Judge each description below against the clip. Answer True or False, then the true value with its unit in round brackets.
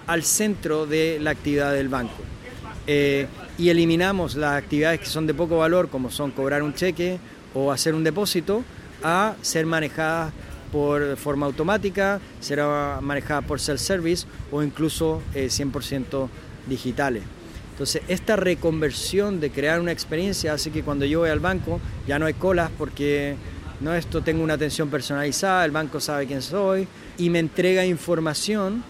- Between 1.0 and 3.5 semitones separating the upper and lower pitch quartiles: True (3.2 semitones)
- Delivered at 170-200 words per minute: False (160 wpm)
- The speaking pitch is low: False (155 Hz)